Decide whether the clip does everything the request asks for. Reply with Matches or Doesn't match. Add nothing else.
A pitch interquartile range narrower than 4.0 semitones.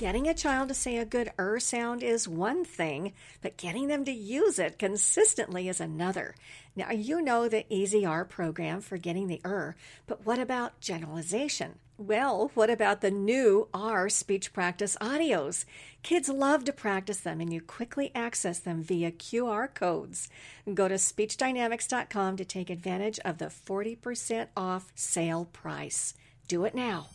Doesn't match